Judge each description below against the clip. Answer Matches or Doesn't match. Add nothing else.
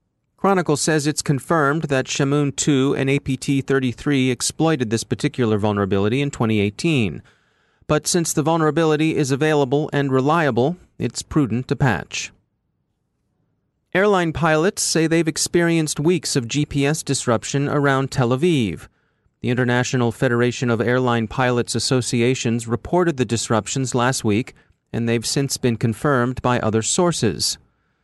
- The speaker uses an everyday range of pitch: Matches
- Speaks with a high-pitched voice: Doesn't match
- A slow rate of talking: Matches